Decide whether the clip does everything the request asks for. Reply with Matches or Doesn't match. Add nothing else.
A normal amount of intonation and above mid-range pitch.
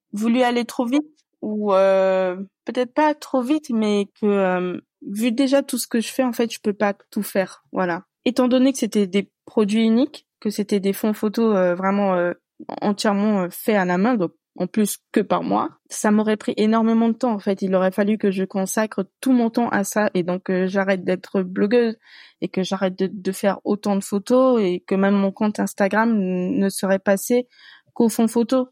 Matches